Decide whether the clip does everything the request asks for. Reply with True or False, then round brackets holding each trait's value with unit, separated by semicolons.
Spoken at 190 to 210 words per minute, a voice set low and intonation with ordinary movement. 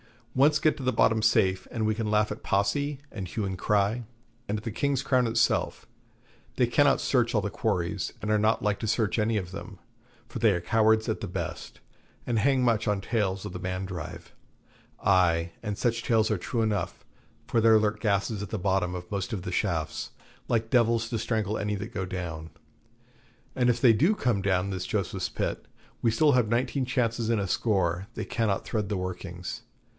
True (200 wpm; 105 Hz; 3.2 semitones)